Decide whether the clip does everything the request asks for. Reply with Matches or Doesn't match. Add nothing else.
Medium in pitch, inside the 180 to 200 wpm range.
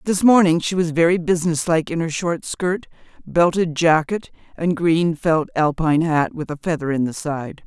Matches